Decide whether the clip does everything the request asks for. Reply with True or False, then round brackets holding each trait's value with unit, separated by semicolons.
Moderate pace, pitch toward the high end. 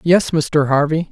False (160 wpm; 155 Hz)